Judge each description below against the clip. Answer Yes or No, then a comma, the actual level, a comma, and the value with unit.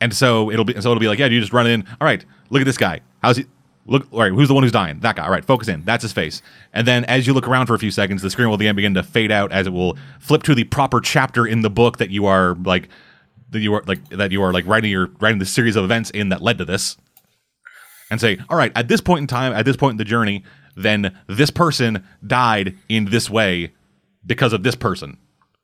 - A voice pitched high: No, low, 115 Hz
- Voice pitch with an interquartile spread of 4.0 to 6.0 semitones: Yes, average, 4.3 semitones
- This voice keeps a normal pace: No, fast, 275 wpm